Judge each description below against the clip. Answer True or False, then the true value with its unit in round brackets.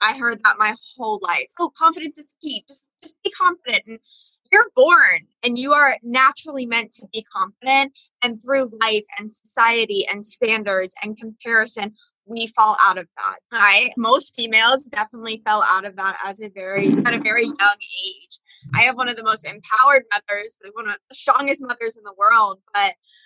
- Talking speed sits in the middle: True (190 wpm)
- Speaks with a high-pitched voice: True (230 Hz)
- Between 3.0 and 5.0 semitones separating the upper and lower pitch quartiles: True (4.5 semitones)